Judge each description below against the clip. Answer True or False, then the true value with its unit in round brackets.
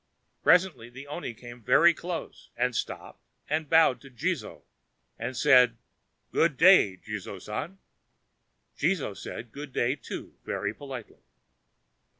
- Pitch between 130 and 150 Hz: True (135 Hz)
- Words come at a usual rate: False (125 wpm)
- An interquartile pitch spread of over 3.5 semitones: True (5.1 semitones)